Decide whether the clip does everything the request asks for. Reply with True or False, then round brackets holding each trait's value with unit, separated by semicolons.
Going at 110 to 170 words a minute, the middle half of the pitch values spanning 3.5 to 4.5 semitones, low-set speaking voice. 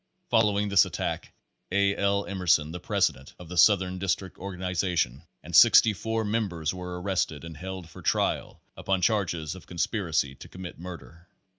False (160 wpm; 2.8 semitones; 90 Hz)